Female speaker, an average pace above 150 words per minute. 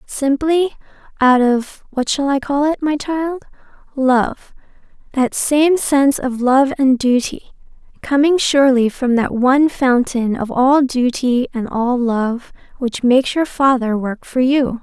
No: female; average, 140 wpm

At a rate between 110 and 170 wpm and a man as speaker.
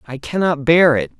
No: average, 200 wpm; male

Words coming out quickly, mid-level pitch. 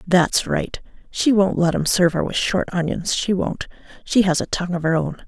Yes: fast, 225 wpm; medium, 180 Hz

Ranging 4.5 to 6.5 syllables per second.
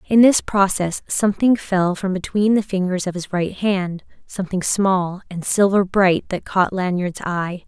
No: 4.3 syllables/s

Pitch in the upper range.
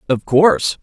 No: medium, 155 Hz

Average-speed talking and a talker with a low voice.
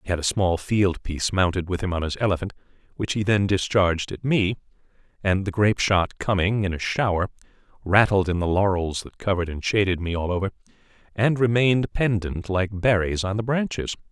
Yes: average, 190 wpm; low, 100 Hz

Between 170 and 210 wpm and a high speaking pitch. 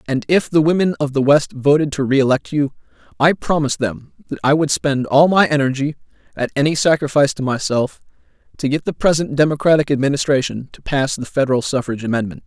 No: average, 185 wpm; medium, 140 Hz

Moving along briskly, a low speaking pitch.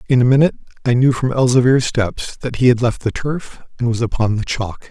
Yes: fast, 230 wpm; low, 125 Hz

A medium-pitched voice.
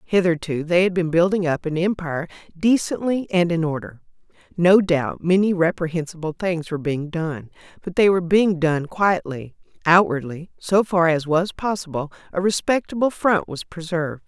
Yes: medium, 170 Hz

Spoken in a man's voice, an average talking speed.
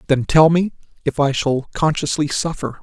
Yes: male; average, 170 wpm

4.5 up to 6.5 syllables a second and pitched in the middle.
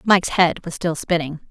Yes: 5.5 syllables/s; medium, 170 Hz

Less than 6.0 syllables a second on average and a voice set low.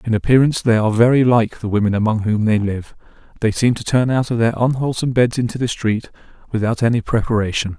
No: 6.5 syllables/s; low, 115 Hz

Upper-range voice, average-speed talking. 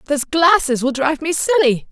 Yes: very high, 295 Hz; average, 190 wpm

